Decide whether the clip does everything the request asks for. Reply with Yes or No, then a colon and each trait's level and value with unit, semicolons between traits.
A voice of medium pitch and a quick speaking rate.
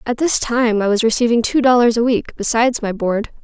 No: high, 230 Hz; fast, 225 wpm